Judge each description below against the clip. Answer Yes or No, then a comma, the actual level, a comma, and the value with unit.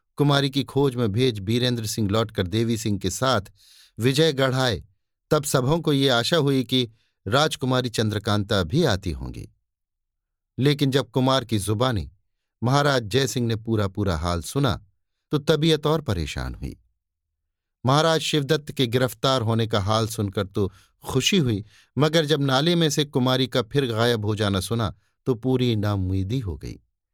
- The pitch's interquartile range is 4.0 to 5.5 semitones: Yes, average, 5.2 semitones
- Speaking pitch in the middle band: No, low, 115 Hz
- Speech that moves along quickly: No, average, 160 wpm